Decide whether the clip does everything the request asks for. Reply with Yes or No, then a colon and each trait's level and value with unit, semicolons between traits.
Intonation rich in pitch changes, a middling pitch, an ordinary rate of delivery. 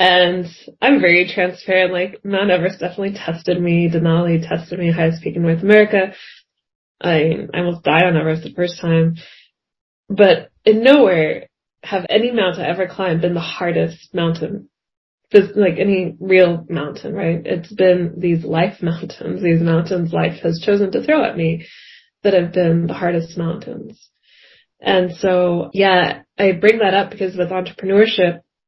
No: narrow, 2.5 semitones; medium, 180 Hz; average, 155 wpm